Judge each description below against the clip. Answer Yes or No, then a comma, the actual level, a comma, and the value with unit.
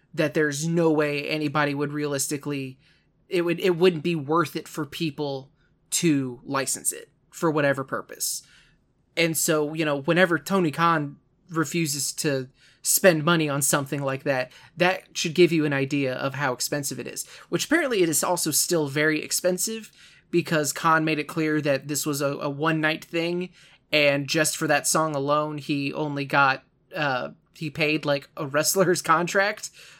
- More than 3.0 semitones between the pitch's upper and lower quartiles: No, average, 2.7 semitones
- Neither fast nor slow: Yes, average, 170 wpm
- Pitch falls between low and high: Yes, medium, 155 Hz